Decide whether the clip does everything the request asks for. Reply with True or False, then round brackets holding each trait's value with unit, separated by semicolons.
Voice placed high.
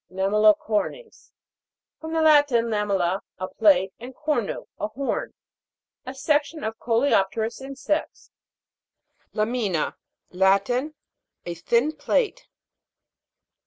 True (230 Hz)